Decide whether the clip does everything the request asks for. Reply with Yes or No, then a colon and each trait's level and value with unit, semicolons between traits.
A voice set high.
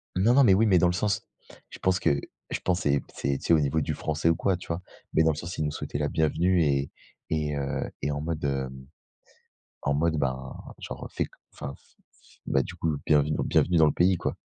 No: very low, 80 Hz